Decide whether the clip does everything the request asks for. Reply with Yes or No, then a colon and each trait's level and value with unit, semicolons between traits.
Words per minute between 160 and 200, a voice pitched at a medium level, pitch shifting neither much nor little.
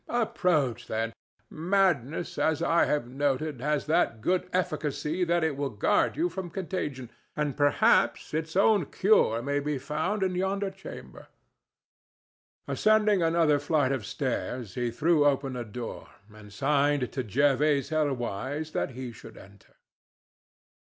No: slow, 135 wpm; medium, 150 Hz; average, 4.8 semitones